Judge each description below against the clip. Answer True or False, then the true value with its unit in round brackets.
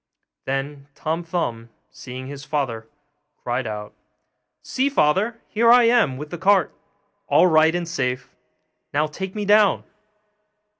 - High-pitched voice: False (155 Hz)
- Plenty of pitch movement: True (6.5 semitones)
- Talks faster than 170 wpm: False (135 wpm)